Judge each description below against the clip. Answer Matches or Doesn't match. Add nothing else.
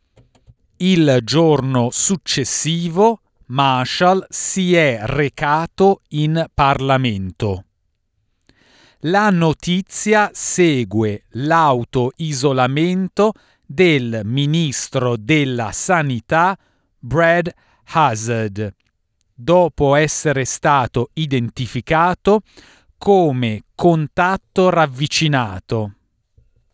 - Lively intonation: Matches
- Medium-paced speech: Doesn't match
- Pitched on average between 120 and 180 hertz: Matches